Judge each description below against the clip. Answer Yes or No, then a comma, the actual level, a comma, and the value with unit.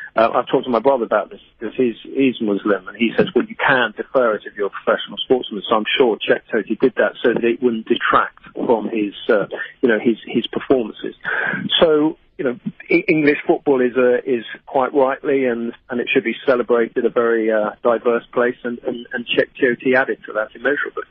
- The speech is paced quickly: Yes, fast, 215 wpm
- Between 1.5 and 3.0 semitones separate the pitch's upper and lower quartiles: Yes, narrow, 2.6 semitones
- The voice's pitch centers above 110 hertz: Yes, low, 120 Hz